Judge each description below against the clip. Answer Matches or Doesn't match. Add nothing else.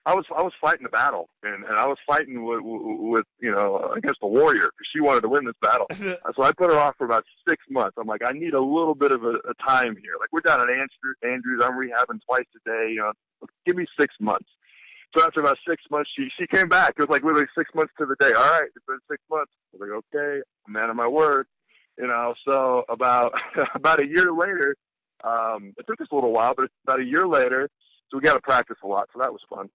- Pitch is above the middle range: Doesn't match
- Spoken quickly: Matches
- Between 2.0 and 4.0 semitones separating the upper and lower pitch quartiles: Doesn't match